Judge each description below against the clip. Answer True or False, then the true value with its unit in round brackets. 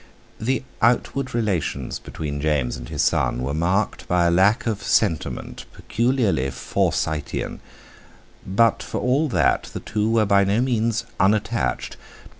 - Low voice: True (100 Hz)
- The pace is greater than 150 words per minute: False (135 wpm)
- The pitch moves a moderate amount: False (6.7 semitones)